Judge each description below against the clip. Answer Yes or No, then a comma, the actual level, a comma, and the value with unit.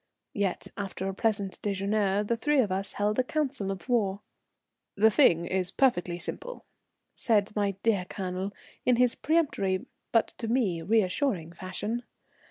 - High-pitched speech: Yes, high, 205 Hz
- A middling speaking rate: Yes, average, 150 wpm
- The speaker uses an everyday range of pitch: Yes, average, 3.7 semitones